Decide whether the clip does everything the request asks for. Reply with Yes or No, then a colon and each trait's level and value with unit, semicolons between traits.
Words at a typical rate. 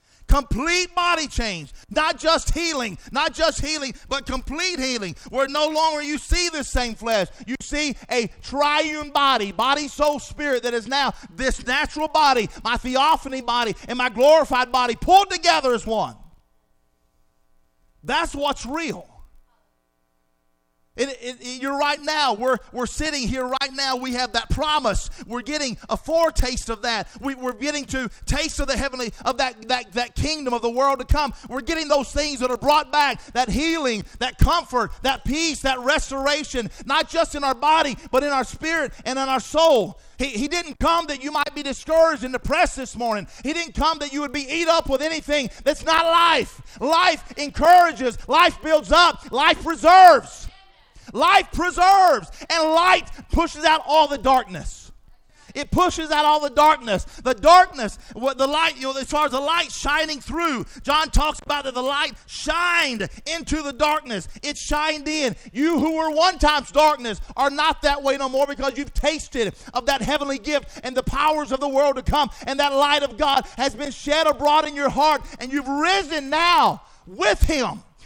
Yes: average, 185 wpm